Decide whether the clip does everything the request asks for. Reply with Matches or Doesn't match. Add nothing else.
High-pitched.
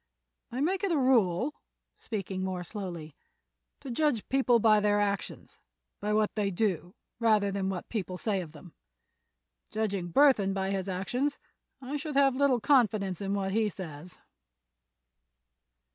Matches